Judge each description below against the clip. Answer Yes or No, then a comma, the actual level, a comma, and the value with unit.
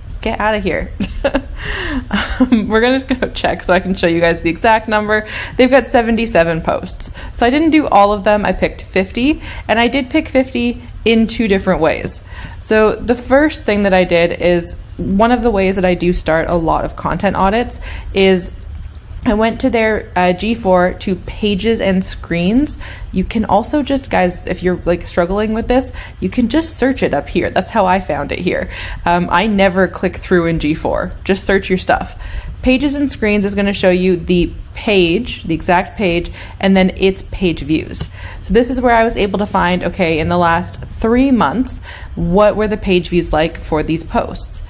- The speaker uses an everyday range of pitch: Yes, average, 4.6 semitones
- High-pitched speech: Yes, high, 195 Hz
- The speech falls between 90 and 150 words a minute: No, fast, 205 wpm